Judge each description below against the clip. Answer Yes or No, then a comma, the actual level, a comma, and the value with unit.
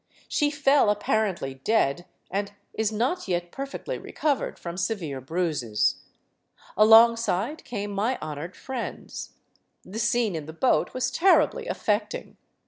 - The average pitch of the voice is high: Yes, high, 210 Hz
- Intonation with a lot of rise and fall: Yes, wide, 6.2 semitones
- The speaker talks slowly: Yes, slow, 125 wpm